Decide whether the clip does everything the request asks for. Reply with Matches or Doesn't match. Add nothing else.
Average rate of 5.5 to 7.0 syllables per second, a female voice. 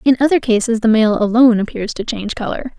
Matches